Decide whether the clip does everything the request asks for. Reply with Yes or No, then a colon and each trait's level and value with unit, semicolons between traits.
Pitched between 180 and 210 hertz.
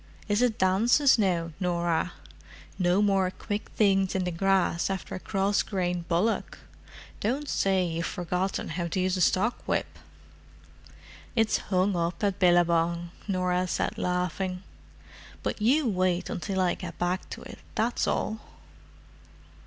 Yes: medium, 185 Hz